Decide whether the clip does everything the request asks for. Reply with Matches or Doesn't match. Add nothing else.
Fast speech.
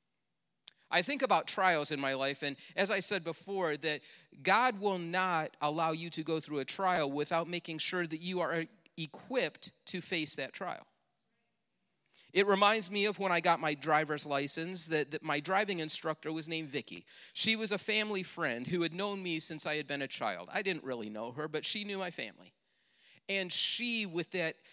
Doesn't match